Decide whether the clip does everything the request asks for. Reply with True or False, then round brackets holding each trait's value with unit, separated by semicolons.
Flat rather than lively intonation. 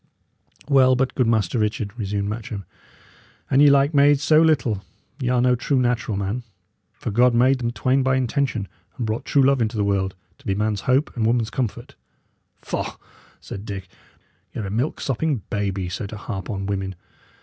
False (4.4 semitones)